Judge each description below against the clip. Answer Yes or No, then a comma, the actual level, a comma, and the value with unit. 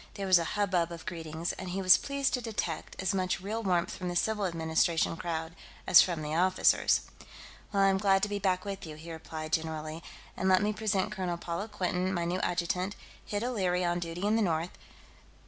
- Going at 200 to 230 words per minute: Yes, fast, 205 wpm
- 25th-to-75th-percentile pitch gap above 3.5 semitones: No, average, 2.7 semitones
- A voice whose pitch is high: No, medium, 180 Hz